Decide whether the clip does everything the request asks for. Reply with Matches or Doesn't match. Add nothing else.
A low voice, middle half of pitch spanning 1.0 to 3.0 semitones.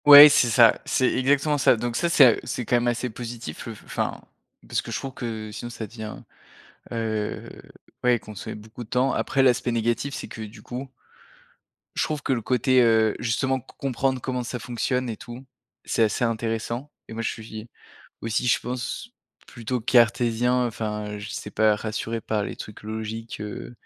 Matches